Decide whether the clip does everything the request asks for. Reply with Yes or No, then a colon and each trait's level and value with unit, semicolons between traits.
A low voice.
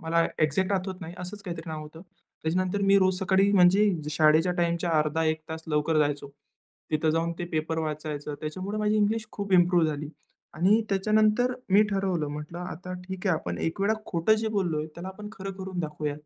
No: medium, 175 Hz